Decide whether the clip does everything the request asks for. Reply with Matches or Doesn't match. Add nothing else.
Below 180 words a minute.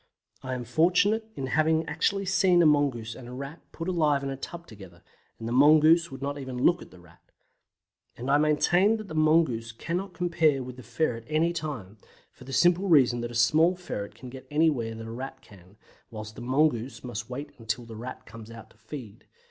Doesn't match